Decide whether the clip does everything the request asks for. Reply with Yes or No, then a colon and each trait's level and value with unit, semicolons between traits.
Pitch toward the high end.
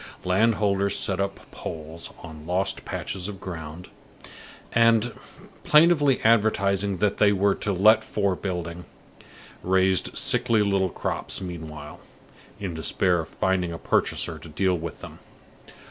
No: very low, 95 Hz